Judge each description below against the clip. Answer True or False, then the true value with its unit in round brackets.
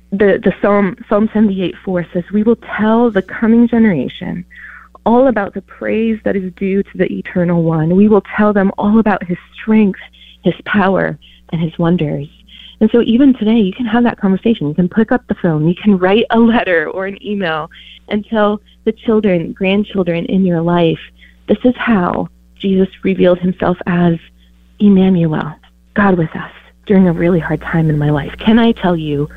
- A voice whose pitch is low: False (190 Hz)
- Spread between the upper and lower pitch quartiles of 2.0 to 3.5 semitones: False (4.1 semitones)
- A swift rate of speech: False (190 wpm)